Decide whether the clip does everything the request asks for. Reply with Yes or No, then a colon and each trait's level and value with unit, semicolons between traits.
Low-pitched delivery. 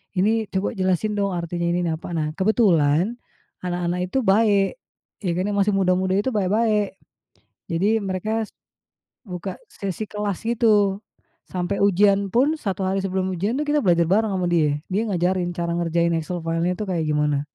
No: high, 190 Hz